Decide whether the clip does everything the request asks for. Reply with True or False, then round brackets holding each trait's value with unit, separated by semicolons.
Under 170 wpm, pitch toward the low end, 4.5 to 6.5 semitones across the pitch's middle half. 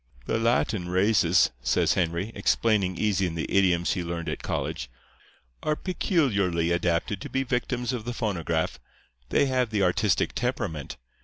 True (150 wpm; 95 Hz; 5.2 semitones)